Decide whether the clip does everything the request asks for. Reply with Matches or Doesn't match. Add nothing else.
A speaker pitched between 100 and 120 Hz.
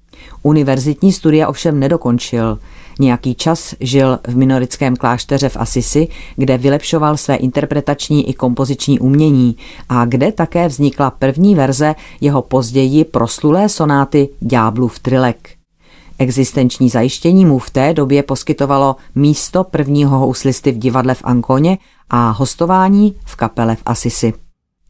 Doesn't match